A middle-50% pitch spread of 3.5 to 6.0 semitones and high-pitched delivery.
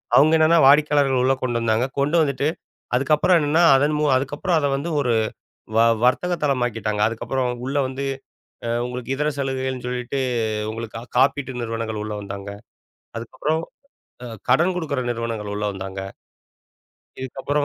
No: average, 4.0 semitones; low, 130 Hz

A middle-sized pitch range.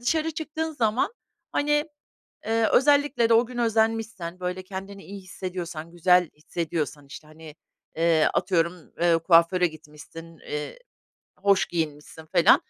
No: wide, 5.7 semitones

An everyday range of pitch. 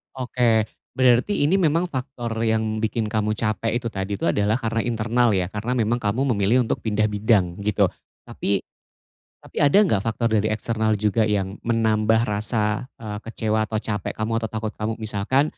No: narrow, 2.0 semitones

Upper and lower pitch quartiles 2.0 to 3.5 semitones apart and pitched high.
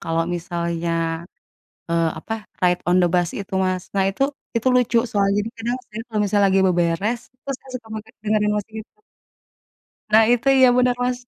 No: average, 4.3 semitones; high, 210 Hz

